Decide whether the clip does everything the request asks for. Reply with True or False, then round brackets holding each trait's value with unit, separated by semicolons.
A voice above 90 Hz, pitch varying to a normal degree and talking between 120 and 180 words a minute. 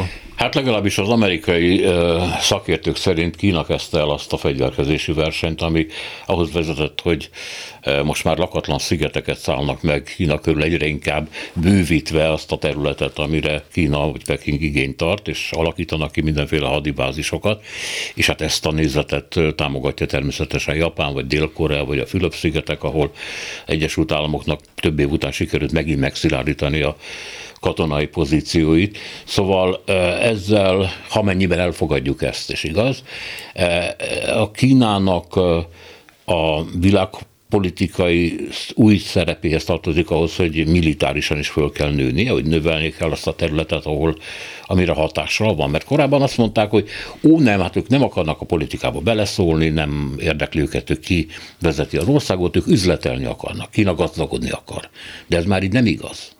False (85 Hz; 3.7 semitones; 145 wpm)